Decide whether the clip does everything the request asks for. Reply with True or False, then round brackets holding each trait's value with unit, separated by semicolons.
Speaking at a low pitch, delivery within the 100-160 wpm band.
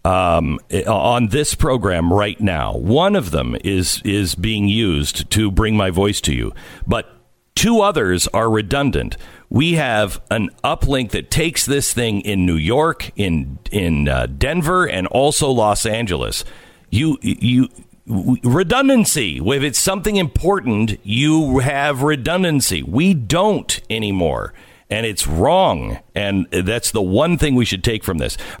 True (110 Hz; 145 wpm)